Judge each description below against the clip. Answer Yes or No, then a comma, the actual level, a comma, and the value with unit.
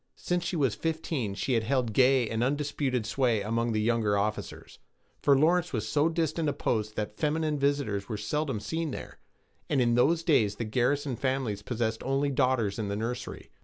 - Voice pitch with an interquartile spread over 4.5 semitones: Yes, average, 4.9 semitones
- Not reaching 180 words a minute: No, average, 185 wpm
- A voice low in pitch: Yes, low, 125 Hz